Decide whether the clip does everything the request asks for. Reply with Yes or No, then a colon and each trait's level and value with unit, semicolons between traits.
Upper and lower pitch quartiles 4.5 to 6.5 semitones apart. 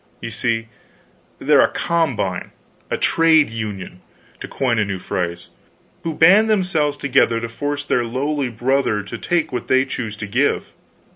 Yes: average, 5.3 semitones